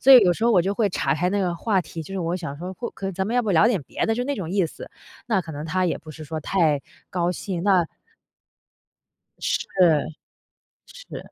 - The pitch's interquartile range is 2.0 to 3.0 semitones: No, average, 3.7 semitones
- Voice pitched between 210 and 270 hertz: No, medium, 185 Hz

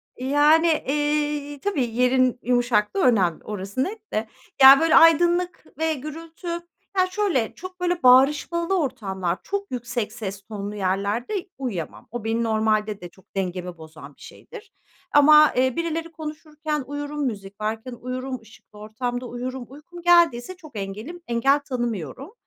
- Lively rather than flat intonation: Yes, wide, 6.4 semitones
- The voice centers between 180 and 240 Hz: No, very high, 255 Hz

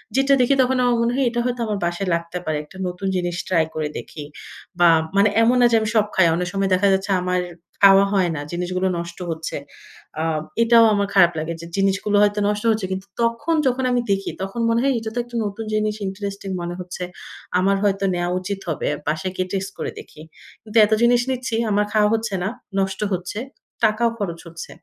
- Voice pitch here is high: Yes, high, 195 Hz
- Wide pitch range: No, average, 3.8 semitones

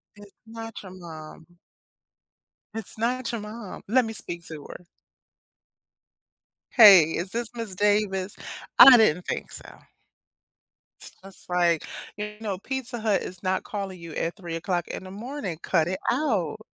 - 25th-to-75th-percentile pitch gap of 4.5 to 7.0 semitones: No, average, 4.0 semitones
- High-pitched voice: Yes, high, 195 Hz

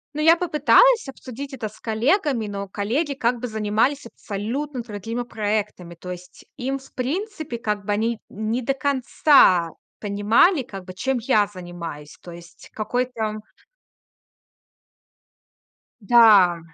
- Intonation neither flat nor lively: Yes, average, 4.8 semitones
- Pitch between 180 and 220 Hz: No, high, 230 Hz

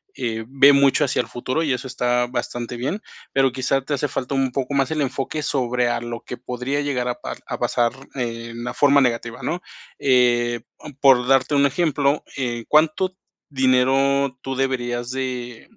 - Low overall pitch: Yes, low, 130 Hz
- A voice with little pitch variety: Yes, narrow, 2.2 semitones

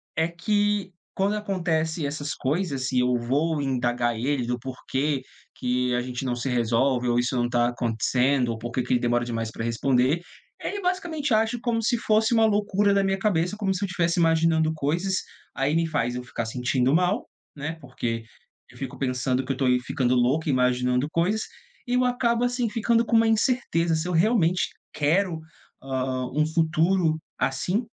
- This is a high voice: No, medium, 155 Hz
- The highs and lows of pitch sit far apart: Yes, wide, 7.6 semitones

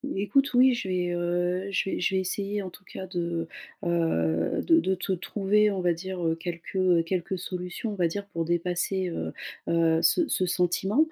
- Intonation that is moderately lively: No, narrow, 2.2 semitones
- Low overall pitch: No, medium, 180 Hz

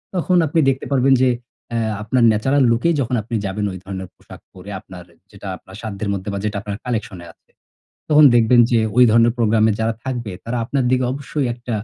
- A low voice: Yes, low, 115 Hz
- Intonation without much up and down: No, average, 4.0 semitones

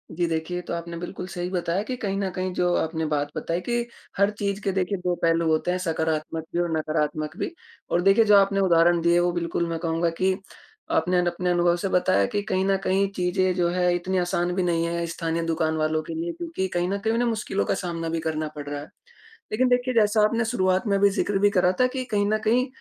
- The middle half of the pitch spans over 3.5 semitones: No, average, 3.0 semitones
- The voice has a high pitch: No, medium, 180 Hz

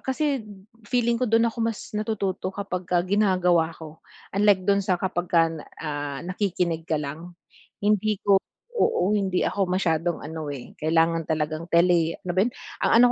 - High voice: No, medium, 180 Hz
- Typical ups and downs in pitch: Yes, average, 3.9 semitones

